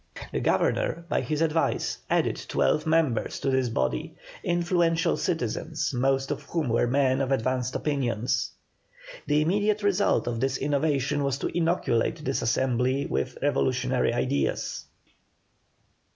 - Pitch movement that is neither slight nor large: Yes, average, 3.8 semitones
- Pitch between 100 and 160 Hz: Yes, medium, 140 Hz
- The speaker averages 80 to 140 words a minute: Yes, slow, 135 wpm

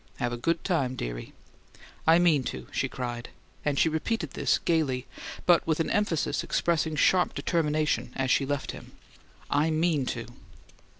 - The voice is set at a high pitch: No, medium, 155 Hz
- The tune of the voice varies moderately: Yes, average, 4.2 semitones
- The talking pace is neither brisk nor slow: Yes, average, 160 wpm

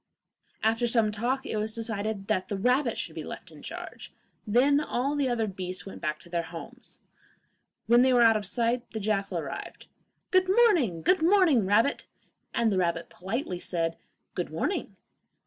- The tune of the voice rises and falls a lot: No, average, 4.7 semitones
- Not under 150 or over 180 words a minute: Yes, average, 175 wpm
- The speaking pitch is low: No, high, 225 Hz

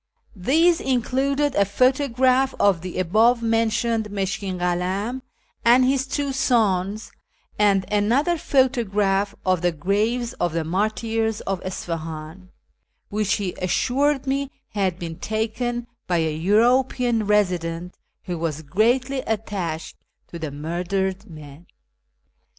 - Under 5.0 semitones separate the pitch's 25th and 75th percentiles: No, wide, 5.4 semitones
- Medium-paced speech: No, slow, 120 wpm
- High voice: Yes, high, 210 Hz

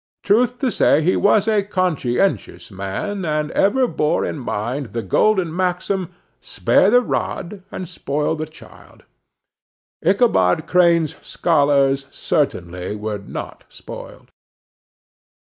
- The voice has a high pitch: No, medium, 165 Hz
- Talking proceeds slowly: Yes, slow, 115 wpm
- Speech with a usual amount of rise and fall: No, wide, 6.4 semitones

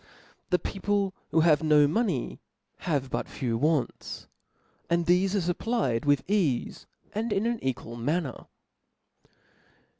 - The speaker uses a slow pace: Yes, slow, 125 wpm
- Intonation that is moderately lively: No, wide, 6.1 semitones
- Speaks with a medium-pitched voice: Yes, medium, 165 Hz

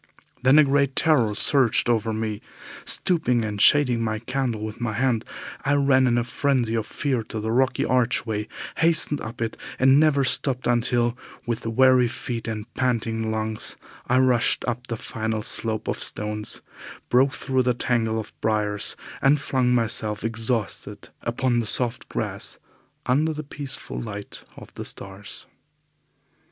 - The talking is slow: No, average, 155 wpm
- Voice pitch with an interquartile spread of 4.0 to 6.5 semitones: No, average, 3.0 semitones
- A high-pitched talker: No, low, 120 Hz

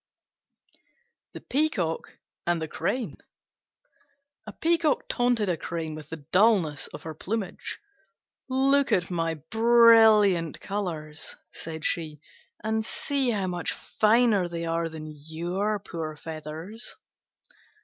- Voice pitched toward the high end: No, medium, 180 Hz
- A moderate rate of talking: No, slow, 115 wpm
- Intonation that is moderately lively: No, wide, 5.7 semitones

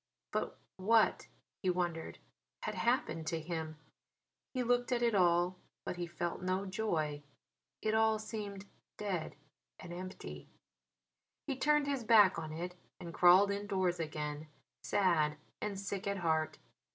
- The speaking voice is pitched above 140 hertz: Yes, medium, 185 Hz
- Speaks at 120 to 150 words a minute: Yes, average, 140 wpm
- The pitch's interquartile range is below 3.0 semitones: No, average, 4.2 semitones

